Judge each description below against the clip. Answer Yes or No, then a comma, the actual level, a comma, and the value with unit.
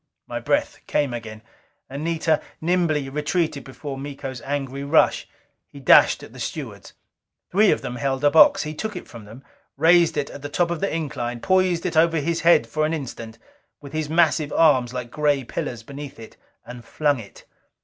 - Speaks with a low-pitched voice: No, medium, 145 Hz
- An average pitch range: Yes, average, 3.7 semitones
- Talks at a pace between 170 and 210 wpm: Yes, average, 180 wpm